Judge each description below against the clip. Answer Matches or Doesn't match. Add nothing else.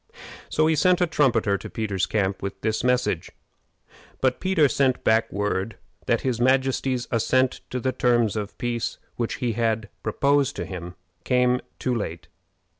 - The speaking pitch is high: Doesn't match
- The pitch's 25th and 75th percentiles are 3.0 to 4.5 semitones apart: Matches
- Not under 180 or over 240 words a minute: Doesn't match